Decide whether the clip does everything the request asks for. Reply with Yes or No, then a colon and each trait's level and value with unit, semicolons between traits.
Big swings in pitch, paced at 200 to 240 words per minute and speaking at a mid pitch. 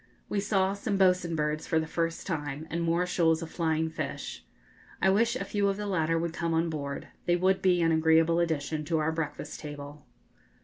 No: narrow, 2.4 semitones; fast, 205 wpm; medium, 165 Hz